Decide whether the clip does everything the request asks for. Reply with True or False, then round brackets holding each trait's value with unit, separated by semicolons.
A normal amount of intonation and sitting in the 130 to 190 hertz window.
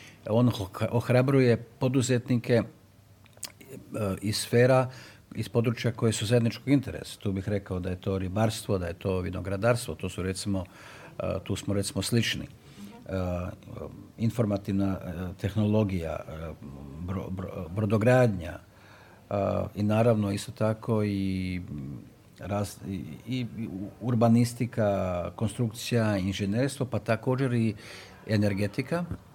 False (3.5 semitones; 105 Hz)